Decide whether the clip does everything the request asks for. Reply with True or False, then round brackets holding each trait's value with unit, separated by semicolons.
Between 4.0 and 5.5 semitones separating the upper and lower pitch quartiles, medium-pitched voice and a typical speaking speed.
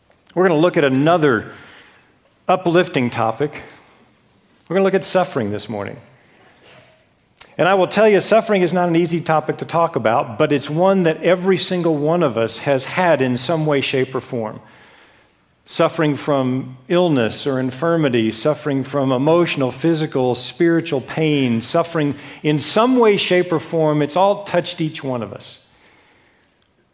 True (4.9 semitones; 150 Hz; 160 wpm)